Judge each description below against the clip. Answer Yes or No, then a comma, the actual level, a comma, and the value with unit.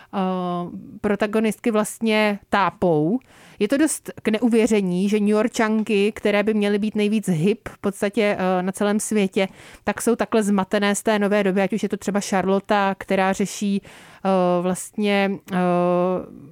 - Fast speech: No, average, 140 wpm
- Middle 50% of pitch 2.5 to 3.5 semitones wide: No, narrow, 2.0 semitones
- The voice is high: Yes, high, 205 Hz